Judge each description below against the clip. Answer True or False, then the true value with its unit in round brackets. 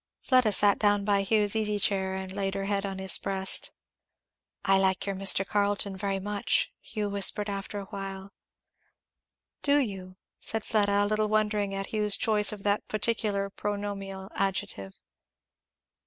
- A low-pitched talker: False (200 Hz)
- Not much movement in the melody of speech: True (1.3 semitones)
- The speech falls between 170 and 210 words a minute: False (150 wpm)